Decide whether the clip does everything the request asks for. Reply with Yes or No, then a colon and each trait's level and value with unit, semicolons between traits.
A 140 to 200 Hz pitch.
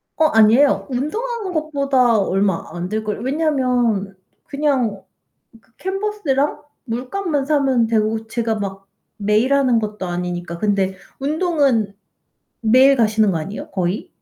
No: high, 235 Hz